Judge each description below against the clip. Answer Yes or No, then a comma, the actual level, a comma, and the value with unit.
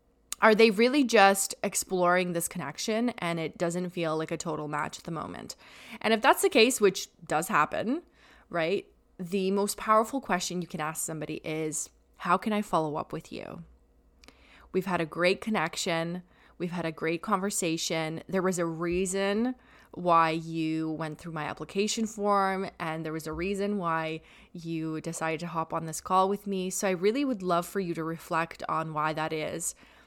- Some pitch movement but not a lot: Yes, average, 3.8 semitones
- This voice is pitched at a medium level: Yes, medium, 175 Hz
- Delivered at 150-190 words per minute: Yes, average, 185 wpm